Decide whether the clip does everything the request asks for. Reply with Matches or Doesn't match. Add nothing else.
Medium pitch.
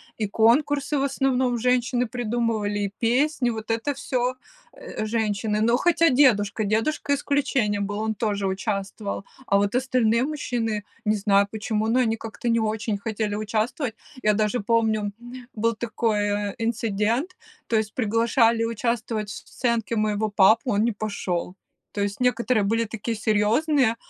Doesn't match